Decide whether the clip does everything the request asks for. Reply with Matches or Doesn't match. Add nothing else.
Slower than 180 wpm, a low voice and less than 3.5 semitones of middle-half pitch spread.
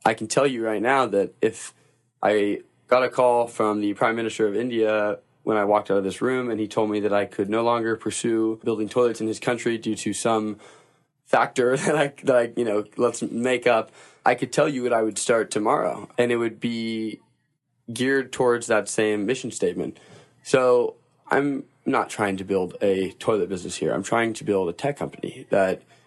Doesn't match